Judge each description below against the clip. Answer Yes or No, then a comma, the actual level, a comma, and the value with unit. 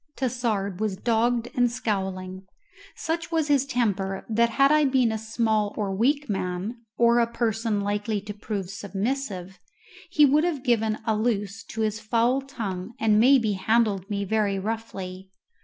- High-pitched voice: Yes, high, 220 Hz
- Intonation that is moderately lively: Yes, average, 3.3 semitones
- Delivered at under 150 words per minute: No, average, 155 wpm